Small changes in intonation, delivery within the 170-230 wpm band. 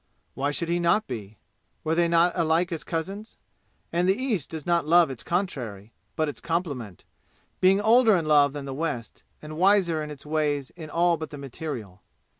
No: average, 3.5 semitones; average, 190 wpm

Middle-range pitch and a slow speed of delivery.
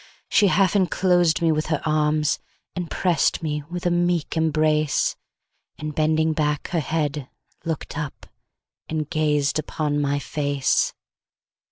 Yes: medium, 155 Hz; slow, 120 wpm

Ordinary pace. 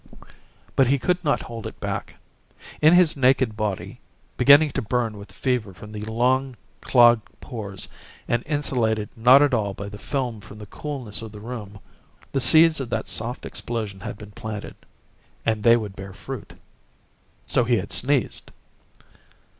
Yes: average, 160 wpm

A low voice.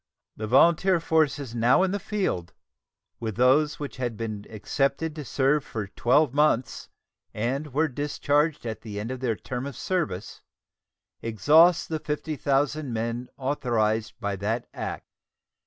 Yes: low, 130 Hz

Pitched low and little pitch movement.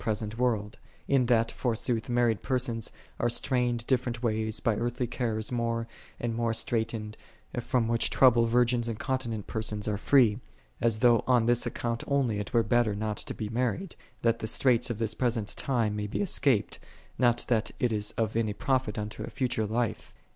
Yes: low, 115 Hz; narrow, 2.0 semitones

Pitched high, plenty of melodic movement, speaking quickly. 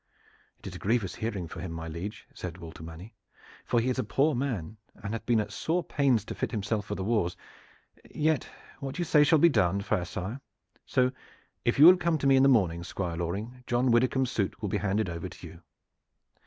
No: low, 110 Hz; wide, 6.1 semitones; fast, 220 wpm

